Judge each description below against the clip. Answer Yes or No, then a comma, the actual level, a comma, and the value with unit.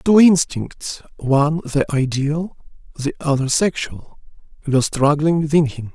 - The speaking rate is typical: No, slow, 100 wpm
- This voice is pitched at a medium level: Yes, medium, 145 Hz